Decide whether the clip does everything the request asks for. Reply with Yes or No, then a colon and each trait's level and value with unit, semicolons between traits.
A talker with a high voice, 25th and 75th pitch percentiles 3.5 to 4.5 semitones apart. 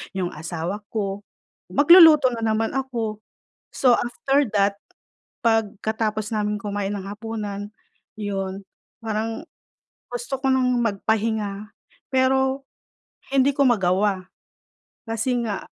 Yes: high, 220 Hz; average, 3.8 semitones